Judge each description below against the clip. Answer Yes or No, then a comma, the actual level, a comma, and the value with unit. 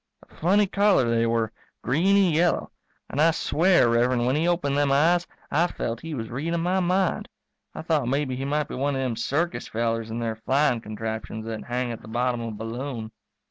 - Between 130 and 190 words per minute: No, fast, 205 wpm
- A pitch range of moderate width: No, wide, 6.1 semitones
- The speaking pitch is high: No, low, 135 Hz